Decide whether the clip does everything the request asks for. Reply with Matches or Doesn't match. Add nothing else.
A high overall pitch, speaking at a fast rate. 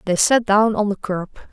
Matches